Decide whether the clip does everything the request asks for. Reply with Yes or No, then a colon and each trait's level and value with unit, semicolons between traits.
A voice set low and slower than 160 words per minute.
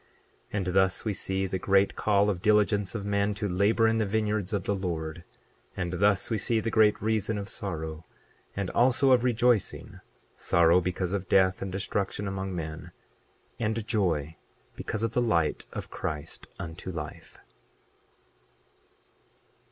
Yes: low, 100 Hz; average, 150 wpm